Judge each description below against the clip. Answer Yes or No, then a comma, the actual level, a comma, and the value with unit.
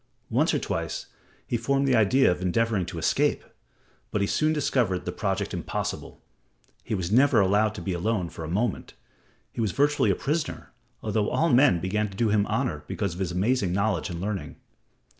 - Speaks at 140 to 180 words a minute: No, average, 190 wpm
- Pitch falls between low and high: No, low, 105 Hz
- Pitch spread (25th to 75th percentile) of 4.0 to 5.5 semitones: Yes, average, 4.5 semitones